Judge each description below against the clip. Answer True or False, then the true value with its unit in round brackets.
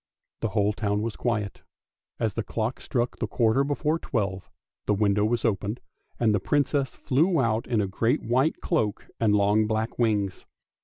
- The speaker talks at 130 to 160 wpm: False (170 wpm)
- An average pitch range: True (3.0 semitones)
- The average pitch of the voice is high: False (110 Hz)